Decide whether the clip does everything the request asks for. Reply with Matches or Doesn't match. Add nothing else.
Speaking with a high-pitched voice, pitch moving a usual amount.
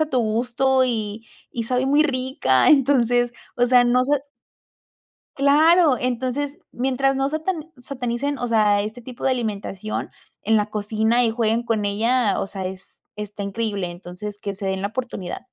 Matches